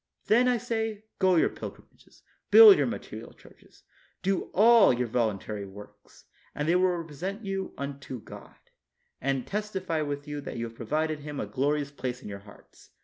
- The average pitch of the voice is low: No, medium, 150 Hz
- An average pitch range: No, wide, 7.3 semitones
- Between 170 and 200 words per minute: Yes, average, 175 wpm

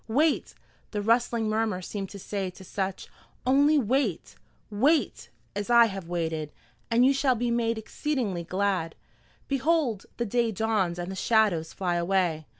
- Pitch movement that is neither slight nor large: Yes, average, 4.6 semitones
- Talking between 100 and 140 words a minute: No, average, 150 wpm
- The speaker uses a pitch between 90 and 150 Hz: No, high, 215 Hz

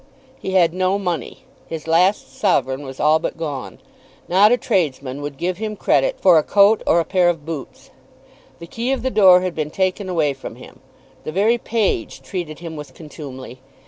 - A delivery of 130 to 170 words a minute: No, average, 190 wpm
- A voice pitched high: No, medium, 170 Hz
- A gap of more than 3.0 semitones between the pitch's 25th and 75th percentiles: Yes, average, 4.6 semitones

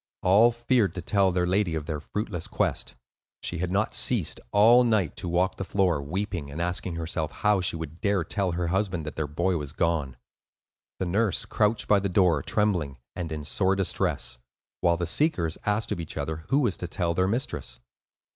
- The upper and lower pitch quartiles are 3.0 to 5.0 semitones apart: Yes, average, 3.8 semitones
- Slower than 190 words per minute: No, average, 195 wpm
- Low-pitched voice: Yes, very low, 90 Hz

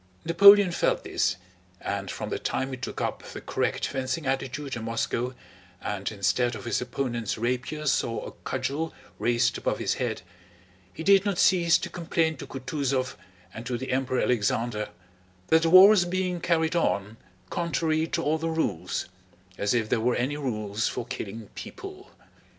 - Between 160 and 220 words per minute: Yes, average, 165 wpm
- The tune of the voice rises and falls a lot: Yes, wide, 6.0 semitones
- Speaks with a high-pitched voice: No, low, 130 Hz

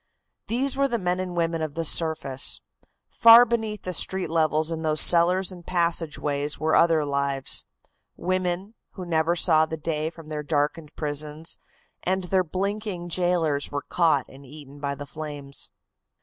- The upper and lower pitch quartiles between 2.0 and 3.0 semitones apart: No, average, 3.4 semitones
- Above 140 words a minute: Yes, average, 160 wpm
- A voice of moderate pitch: Yes, medium, 165 Hz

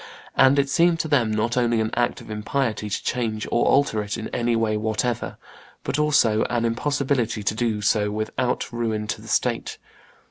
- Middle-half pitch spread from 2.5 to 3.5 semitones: Yes, average, 2.9 semitones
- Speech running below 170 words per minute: No, average, 185 wpm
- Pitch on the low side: Yes, low, 115 Hz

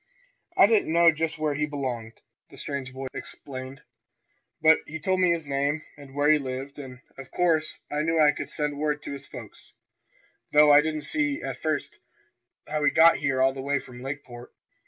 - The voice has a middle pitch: Yes, medium, 145 Hz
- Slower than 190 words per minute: No, average, 195 wpm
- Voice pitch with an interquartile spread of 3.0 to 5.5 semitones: No, narrow, 2.5 semitones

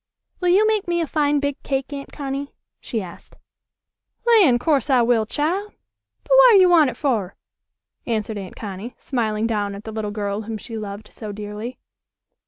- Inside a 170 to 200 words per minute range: Yes, average, 180 wpm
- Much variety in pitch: Yes, wide, 6.0 semitones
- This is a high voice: Yes, high, 240 Hz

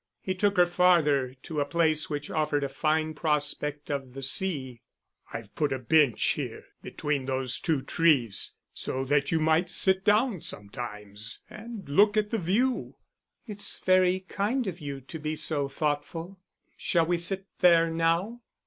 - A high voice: No, medium, 155 Hz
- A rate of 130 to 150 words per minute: No, average, 160 wpm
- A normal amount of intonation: Yes, average, 4.8 semitones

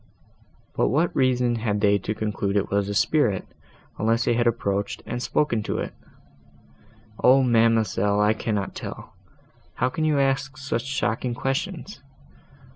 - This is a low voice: Yes, low, 115 Hz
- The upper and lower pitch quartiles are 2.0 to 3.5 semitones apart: No, average, 4.2 semitones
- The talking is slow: No, average, 145 wpm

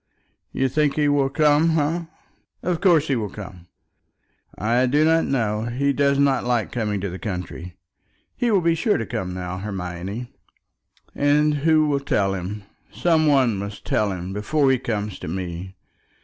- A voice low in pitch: Yes, low, 125 Hz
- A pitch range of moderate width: No, wide, 7.0 semitones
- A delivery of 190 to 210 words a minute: No, average, 170 wpm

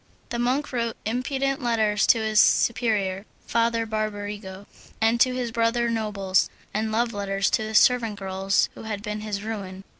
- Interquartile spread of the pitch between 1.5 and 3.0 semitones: Yes, narrow, 2.4 semitones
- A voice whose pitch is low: No, high, 220 Hz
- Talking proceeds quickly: No, average, 160 wpm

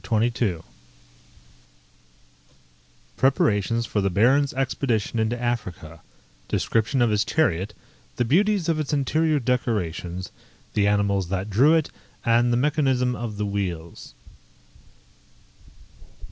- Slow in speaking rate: Yes, slow, 110 wpm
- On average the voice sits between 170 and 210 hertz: No, low, 115 Hz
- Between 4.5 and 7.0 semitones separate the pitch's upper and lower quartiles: Yes, average, 4.8 semitones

